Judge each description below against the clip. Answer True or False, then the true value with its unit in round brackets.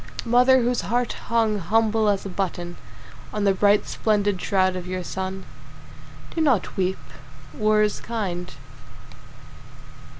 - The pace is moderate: False (130 wpm)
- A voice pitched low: False (205 Hz)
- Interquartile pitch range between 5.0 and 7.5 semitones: False (3.1 semitones)